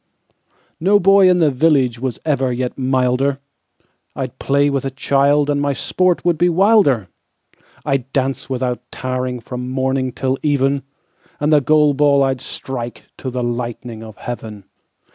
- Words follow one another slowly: Yes, slow, 125 wpm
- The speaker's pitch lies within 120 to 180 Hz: Yes, low, 135 Hz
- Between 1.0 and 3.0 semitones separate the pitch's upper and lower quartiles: Yes, narrow, 2.6 semitones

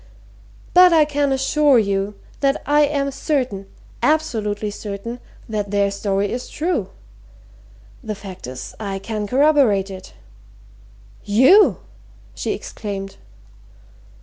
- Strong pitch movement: Yes, wide, 6.2 semitones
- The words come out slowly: Yes, slow, 110 wpm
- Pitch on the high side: Yes, high, 220 Hz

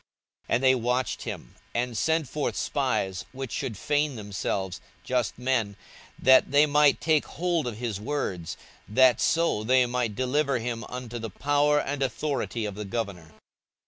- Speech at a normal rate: Yes, average, 160 wpm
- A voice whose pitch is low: Yes, low, 125 Hz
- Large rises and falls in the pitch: No, average, 4.5 semitones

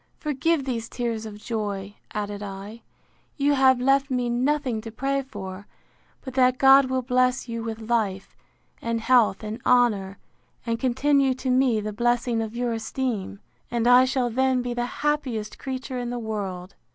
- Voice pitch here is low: No, high, 240 Hz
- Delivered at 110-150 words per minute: No, average, 165 wpm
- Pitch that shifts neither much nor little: Yes, average, 3.0 semitones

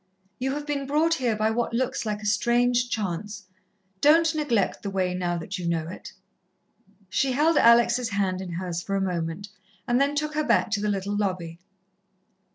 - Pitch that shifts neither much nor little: No, wide, 5.9 semitones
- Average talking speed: Yes, average, 185 wpm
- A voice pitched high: Yes, high, 215 Hz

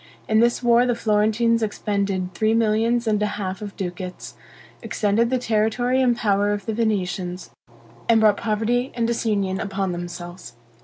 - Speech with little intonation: No, average, 3.1 semitones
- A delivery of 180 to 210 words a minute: No, average, 155 wpm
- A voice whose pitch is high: Yes, high, 210 Hz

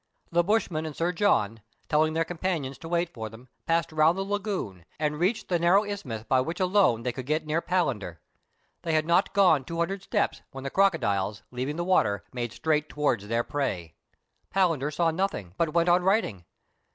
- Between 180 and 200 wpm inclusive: Yes, average, 195 wpm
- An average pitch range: No, wide, 5.9 semitones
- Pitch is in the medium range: Yes, medium, 160 Hz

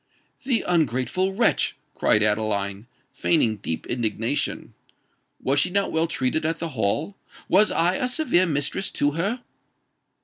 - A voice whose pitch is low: No, medium, 155 Hz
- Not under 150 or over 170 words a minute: No, slow, 135 wpm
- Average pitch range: No, wide, 8.6 semitones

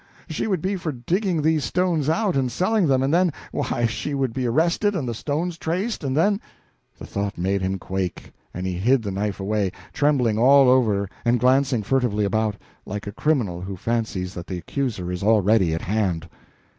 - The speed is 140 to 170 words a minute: No, average, 195 wpm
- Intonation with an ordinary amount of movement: No, wide, 7.4 semitones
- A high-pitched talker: No, low, 120 Hz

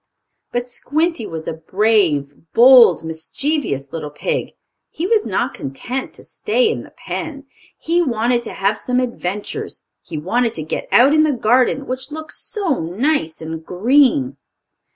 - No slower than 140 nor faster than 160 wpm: Yes, average, 150 wpm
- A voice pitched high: Yes, high, 245 Hz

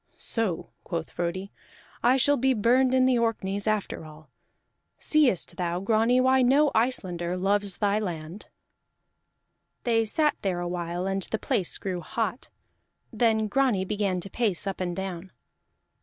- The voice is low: No, high, 205 Hz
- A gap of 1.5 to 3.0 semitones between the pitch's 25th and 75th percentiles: No, average, 4.8 semitones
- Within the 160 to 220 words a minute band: No, average, 145 wpm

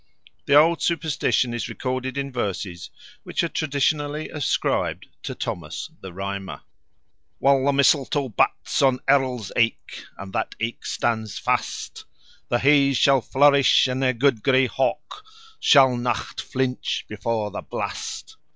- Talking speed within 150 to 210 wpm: No, slow, 135 wpm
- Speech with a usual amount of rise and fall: Yes, average, 3.3 semitones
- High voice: No, low, 130 Hz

